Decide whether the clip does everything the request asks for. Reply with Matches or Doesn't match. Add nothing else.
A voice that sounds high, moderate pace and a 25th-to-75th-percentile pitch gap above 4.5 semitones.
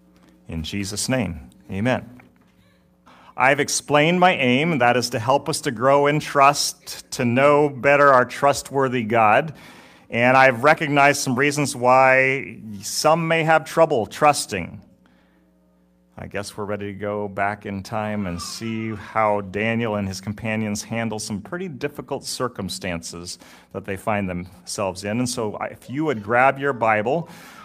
Doesn't match